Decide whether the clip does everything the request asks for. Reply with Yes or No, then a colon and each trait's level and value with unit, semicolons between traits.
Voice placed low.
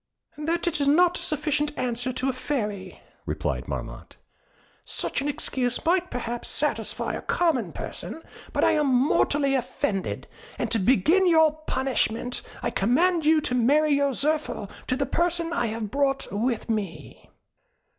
No: very high, 275 Hz